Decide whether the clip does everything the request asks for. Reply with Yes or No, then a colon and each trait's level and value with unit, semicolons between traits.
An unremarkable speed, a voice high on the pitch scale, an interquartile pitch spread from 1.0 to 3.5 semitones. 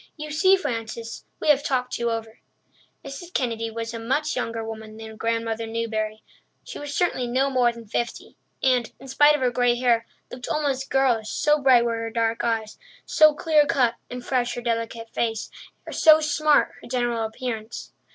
Yes: average, 180 wpm; high, 240 Hz; average, 3.2 semitones